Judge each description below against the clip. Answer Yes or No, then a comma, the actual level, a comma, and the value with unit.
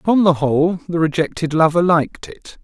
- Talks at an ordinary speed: Yes, average, 180 wpm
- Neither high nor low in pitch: Yes, medium, 165 Hz